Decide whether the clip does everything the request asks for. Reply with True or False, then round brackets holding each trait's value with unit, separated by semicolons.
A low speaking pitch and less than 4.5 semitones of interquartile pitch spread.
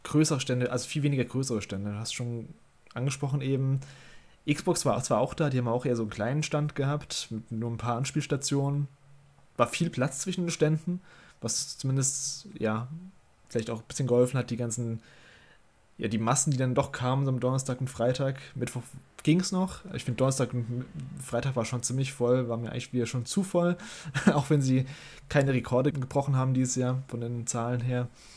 True (130 Hz; 3.0 semitones)